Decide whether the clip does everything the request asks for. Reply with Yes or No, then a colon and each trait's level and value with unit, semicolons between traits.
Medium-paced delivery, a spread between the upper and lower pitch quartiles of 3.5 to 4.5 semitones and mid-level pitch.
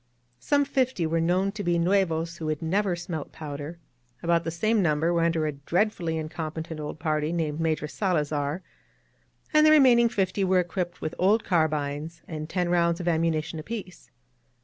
No: average, 170 wpm; average, 3.1 semitones; medium, 170 Hz